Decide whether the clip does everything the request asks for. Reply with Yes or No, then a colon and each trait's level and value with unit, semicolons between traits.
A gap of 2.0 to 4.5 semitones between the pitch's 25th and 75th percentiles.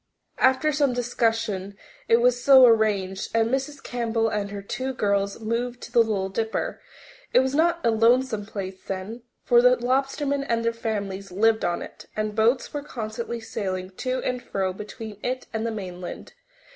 Yes: average, 3.6 semitones